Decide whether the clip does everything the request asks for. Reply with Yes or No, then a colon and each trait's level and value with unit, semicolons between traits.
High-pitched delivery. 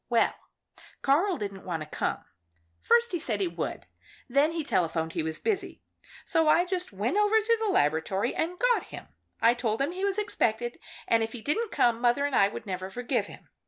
Yes: high, 245 Hz